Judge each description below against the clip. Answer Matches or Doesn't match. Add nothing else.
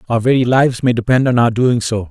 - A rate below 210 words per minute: Doesn't match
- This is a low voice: Matches